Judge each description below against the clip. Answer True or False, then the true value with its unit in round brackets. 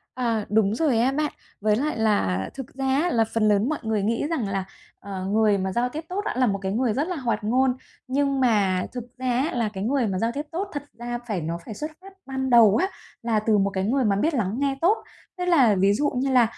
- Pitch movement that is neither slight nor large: True (4.8 semitones)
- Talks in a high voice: True (235 Hz)